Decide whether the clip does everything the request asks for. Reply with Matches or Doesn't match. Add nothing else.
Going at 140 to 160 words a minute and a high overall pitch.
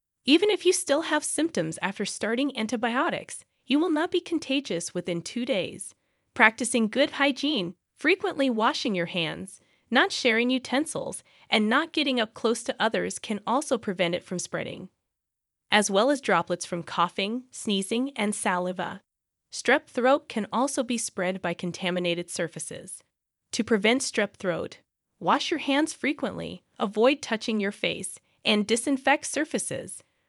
Matches